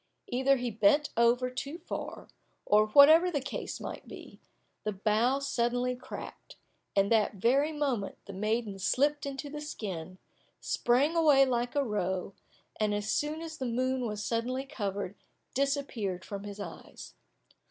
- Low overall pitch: No, high, 245 Hz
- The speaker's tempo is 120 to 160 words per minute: Yes, average, 140 wpm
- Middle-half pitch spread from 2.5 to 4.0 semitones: No, average, 5.0 semitones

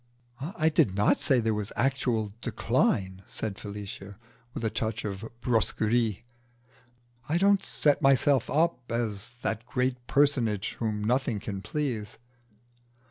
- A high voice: No, low, 115 Hz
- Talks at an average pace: No, slow, 130 wpm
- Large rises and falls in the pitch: No, average, 4.3 semitones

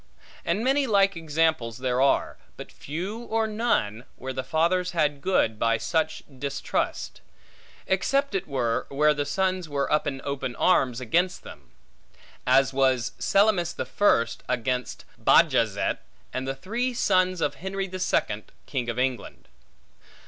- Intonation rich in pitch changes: Yes, wide, 6.6 semitones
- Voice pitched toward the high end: No, medium, 150 Hz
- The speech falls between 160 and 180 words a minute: No, average, 145 wpm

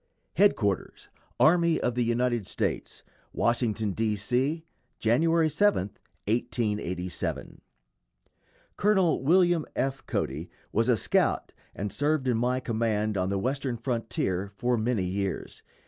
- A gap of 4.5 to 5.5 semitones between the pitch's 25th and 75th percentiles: Yes, average, 4.8 semitones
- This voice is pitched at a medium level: No, low, 120 Hz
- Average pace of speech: No, slow, 120 wpm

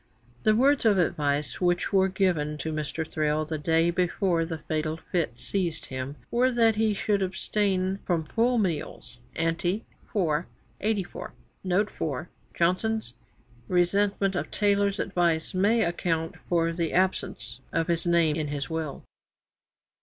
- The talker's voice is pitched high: No, medium, 175 Hz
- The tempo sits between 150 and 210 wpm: No, average, 140 wpm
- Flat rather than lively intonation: No, average, 3.9 semitones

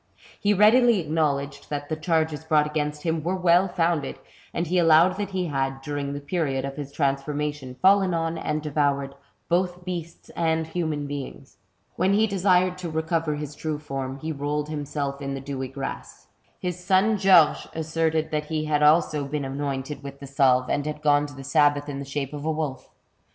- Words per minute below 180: No, average, 190 wpm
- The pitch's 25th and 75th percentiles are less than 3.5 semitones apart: Yes, average, 3.0 semitones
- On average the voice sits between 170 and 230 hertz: No, medium, 150 Hz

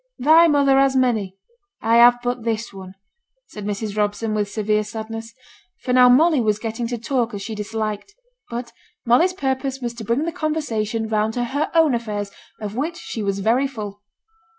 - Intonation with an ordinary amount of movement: Yes, average, 3.7 semitones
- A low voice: No, high, 230 Hz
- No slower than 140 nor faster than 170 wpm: No, average, 180 wpm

